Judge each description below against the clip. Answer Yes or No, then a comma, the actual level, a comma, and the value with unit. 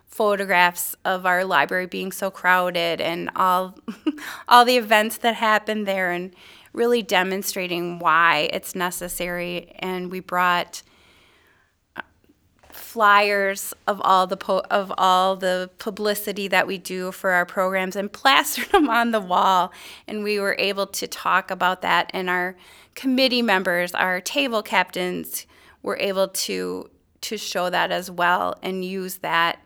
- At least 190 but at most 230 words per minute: No, average, 145 wpm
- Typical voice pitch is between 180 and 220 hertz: Yes, medium, 185 Hz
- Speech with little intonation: Yes, narrow, 2.3 semitones